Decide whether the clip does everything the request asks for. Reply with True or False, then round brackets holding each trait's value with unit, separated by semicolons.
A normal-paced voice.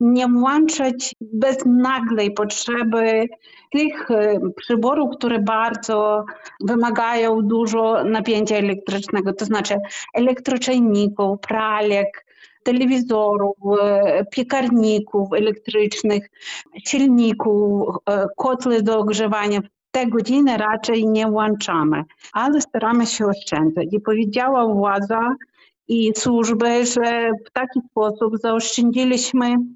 False (85 wpm)